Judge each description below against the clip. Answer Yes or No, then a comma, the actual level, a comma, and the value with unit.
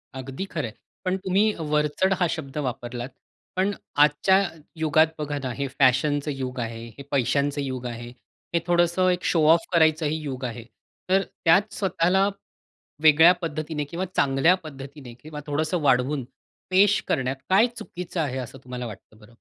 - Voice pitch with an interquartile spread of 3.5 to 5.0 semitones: Yes, average, 4.6 semitones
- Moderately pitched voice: Yes, medium, 150 Hz